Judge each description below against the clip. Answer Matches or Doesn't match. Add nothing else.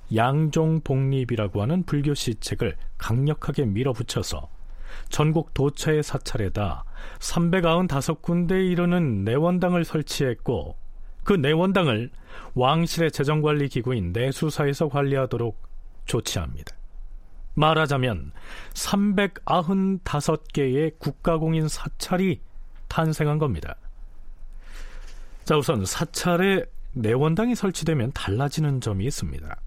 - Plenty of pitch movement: Matches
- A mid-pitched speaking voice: Matches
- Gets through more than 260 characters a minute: Doesn't match